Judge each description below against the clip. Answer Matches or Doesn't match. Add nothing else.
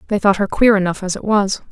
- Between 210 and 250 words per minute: Doesn't match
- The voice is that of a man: Doesn't match